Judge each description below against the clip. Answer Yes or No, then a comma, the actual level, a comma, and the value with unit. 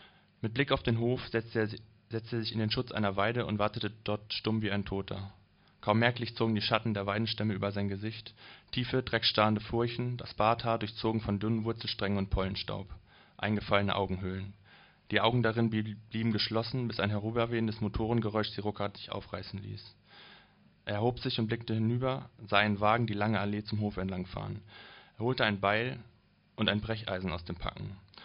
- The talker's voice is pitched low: Yes, low, 110 Hz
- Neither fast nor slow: Yes, average, 170 wpm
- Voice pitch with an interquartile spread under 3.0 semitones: Yes, narrow, 2.4 semitones